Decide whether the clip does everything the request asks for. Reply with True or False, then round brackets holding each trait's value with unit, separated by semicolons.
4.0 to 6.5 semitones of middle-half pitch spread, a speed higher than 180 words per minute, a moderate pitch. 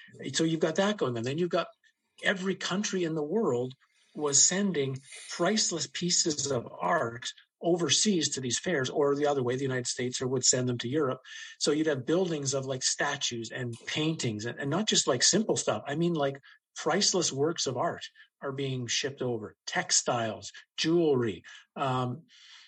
False (5.2 semitones; 175 wpm; 150 Hz)